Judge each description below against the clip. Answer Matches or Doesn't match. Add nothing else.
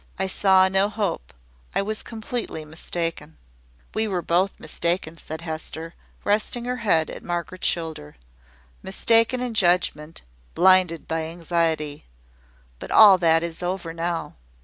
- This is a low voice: Doesn't match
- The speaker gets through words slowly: Matches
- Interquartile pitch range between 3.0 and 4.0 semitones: Matches